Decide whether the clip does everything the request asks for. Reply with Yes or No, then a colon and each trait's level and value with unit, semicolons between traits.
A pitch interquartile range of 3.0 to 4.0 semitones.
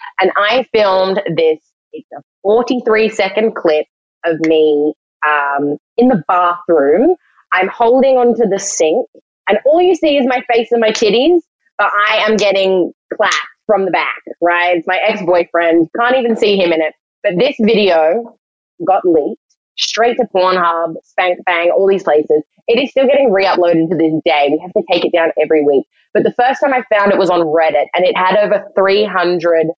No: wide, 5.6 semitones